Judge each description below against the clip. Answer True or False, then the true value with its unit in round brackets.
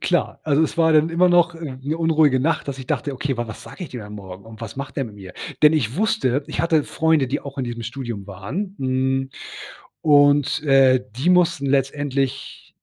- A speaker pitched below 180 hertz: True (140 Hz)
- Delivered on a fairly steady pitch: False (3.9 semitones)